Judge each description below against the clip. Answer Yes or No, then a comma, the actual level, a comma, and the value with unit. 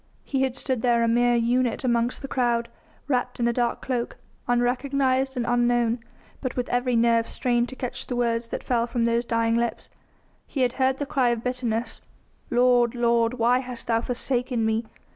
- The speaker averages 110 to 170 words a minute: No, average, 185 wpm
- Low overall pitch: No, high, 240 Hz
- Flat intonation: Yes, narrow, 1.3 semitones